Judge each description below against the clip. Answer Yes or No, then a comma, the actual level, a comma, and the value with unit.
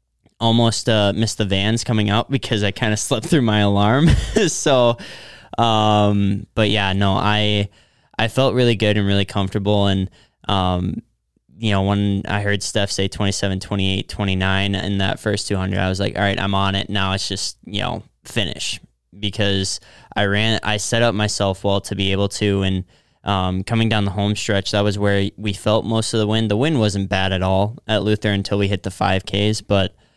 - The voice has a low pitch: Yes, low, 100 Hz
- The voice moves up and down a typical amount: No, narrow, 1.7 semitones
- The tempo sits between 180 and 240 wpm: Yes, average, 200 wpm